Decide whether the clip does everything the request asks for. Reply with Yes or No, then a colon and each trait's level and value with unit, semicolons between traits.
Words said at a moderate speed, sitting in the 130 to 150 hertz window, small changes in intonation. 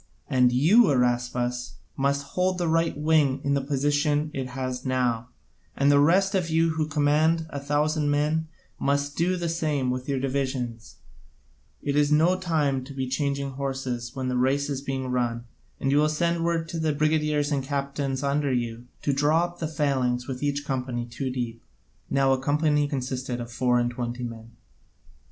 No: average, 185 wpm; medium, 140 Hz; average, 3.0 semitones